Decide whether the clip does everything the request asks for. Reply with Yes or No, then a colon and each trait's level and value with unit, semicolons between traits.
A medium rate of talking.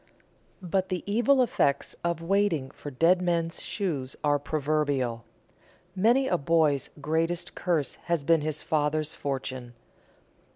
No: slow, 125 wpm